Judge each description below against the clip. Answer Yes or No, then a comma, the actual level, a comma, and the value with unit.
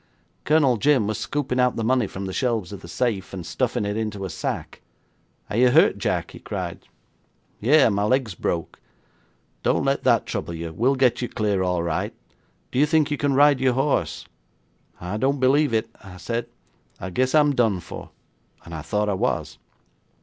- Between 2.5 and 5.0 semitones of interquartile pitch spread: No, wide, 5.4 semitones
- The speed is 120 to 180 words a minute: No, average, 190 wpm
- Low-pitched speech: Yes, low, 115 Hz